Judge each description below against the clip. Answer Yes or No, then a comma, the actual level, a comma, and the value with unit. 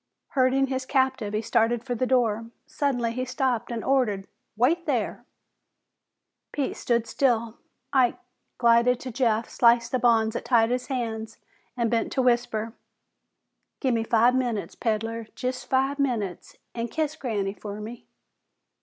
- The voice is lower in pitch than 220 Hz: No, high, 240 Hz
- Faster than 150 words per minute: No, average, 145 wpm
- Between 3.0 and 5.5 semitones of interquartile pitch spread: No, narrow, 2.4 semitones